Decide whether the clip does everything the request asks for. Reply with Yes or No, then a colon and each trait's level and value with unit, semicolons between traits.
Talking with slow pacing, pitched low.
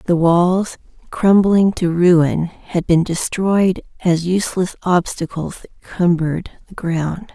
No: slow, 125 wpm; medium, 175 Hz